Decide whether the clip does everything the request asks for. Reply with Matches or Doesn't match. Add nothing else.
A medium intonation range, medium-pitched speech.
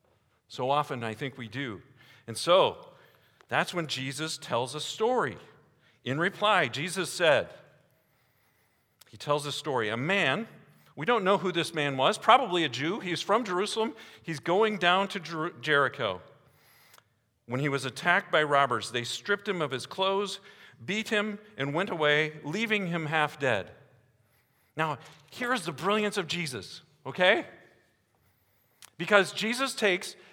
Doesn't match